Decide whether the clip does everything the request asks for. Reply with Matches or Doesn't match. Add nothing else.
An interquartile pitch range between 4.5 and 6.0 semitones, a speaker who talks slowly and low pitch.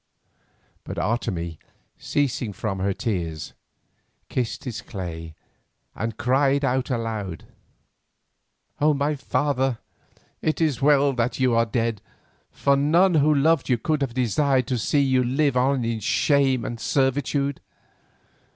Doesn't match